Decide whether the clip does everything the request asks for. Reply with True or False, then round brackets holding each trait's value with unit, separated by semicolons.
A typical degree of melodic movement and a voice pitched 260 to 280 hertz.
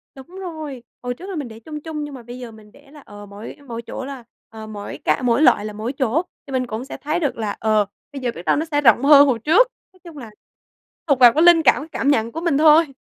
True (4.9 semitones; 265 Hz)